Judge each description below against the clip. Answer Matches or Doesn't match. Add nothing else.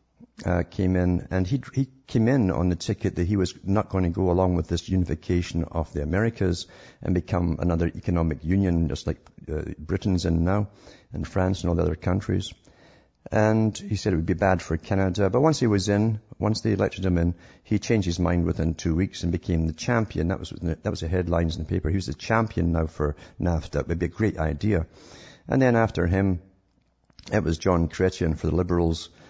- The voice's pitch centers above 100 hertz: Doesn't match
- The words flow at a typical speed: Doesn't match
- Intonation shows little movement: Doesn't match